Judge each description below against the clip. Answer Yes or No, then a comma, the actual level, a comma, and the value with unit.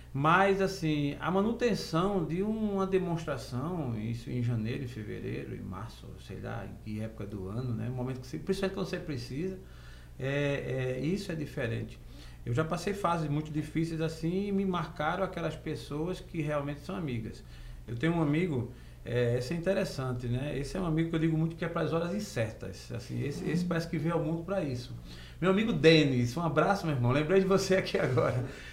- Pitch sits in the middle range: Yes, medium, 155 Hz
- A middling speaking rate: No, fast, 195 wpm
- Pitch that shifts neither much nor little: No, wide, 6.2 semitones